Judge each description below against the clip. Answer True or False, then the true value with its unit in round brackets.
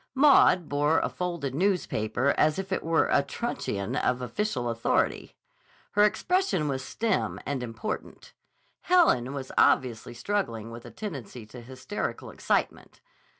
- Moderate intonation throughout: False (8.3 semitones)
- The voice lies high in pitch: False (140 Hz)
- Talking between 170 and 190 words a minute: False (135 wpm)